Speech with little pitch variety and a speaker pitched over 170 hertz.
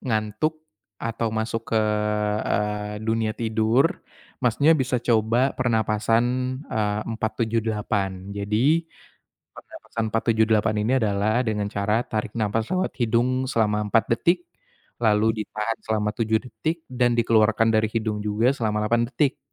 No: narrow, 1.9 semitones; low, 110 Hz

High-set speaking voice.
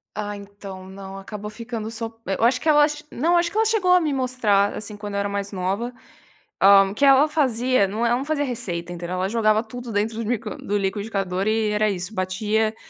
Yes: high, 215 Hz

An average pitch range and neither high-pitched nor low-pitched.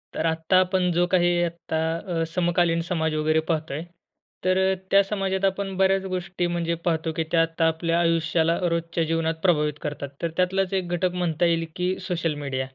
No: narrow, 2.0 semitones; medium, 170 Hz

